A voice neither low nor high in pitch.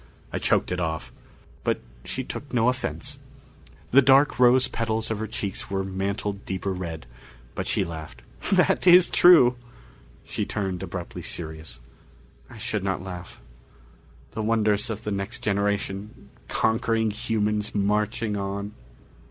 No: low, 105 Hz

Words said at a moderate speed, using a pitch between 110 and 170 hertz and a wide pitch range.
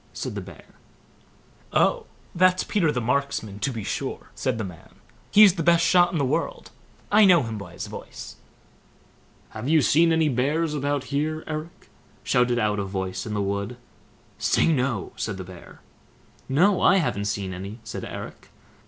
Yes: average, 170 wpm; low, 135 Hz; wide, 8.0 semitones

